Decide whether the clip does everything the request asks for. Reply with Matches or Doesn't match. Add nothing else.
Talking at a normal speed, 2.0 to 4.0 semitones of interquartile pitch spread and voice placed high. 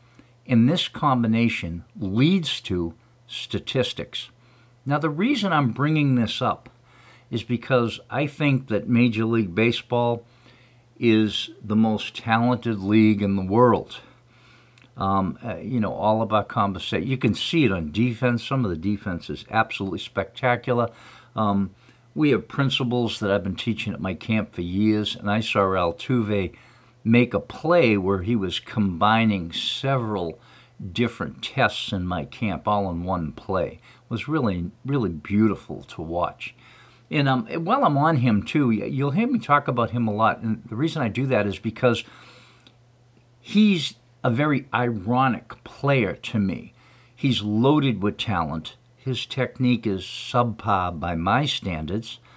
Doesn't match